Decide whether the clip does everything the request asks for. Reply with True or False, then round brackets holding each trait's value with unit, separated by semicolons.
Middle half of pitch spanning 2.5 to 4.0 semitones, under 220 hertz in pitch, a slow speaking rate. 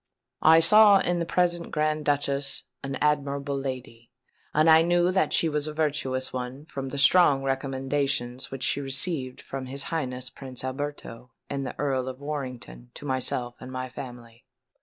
False (2.8 semitones; 140 Hz; 165 wpm)